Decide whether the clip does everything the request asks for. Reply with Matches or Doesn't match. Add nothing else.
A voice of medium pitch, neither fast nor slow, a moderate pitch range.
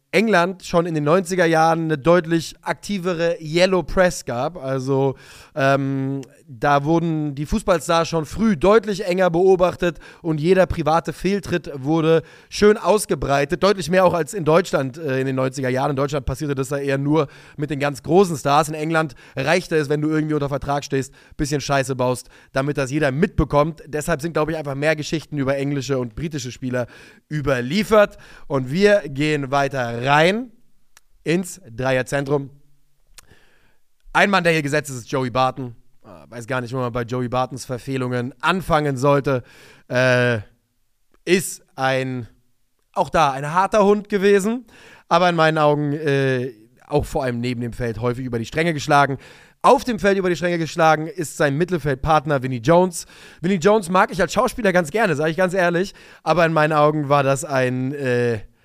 Matches